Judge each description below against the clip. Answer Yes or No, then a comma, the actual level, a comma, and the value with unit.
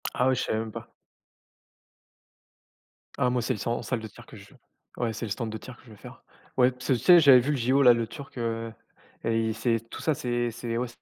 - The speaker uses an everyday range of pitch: No, narrow, 2.0 semitones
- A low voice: Yes, low, 120 Hz